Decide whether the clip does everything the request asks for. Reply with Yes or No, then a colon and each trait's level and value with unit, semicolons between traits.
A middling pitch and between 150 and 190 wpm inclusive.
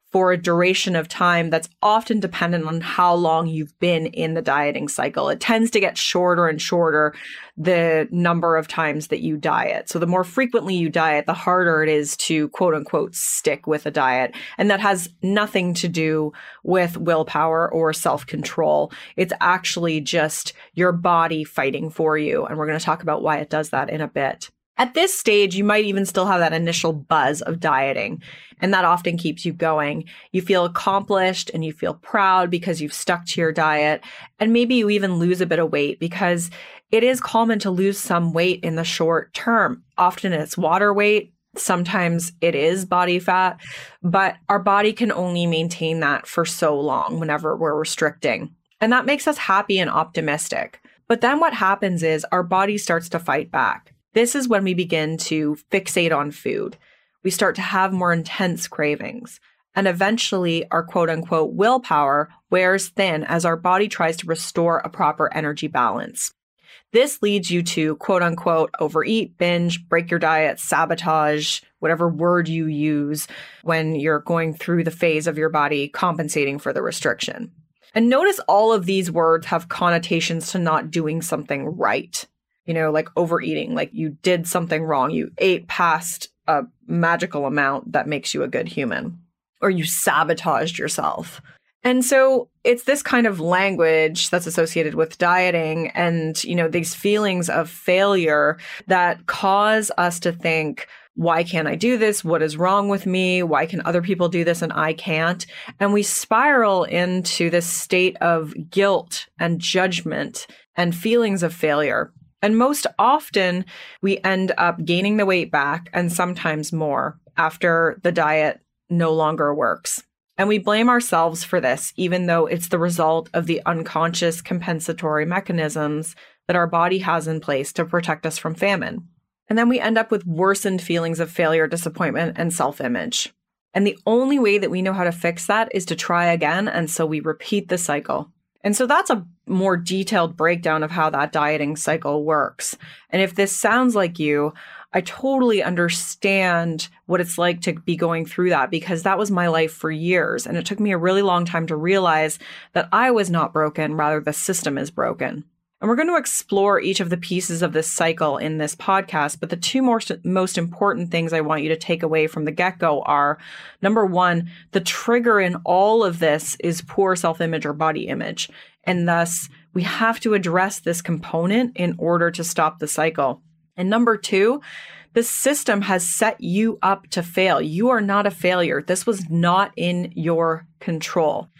Yes: medium, 170 Hz; average, 180 wpm